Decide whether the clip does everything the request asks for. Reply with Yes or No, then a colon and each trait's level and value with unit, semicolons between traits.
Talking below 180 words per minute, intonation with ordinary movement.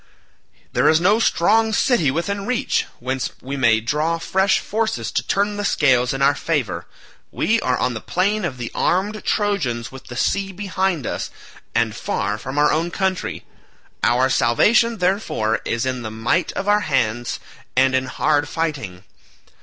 No: average, 165 wpm; wide, 7.9 semitones